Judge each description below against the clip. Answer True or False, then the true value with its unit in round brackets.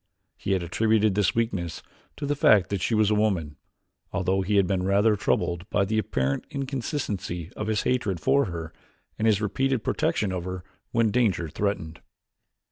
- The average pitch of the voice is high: False (100 Hz)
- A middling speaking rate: True (175 wpm)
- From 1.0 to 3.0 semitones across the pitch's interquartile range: False (3.4 semitones)